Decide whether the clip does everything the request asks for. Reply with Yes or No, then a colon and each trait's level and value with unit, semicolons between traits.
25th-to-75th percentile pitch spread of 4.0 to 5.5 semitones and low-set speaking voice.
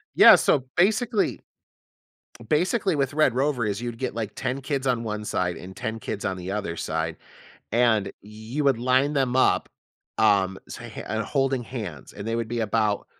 Yes: average, 4.5 semitones; low, 115 Hz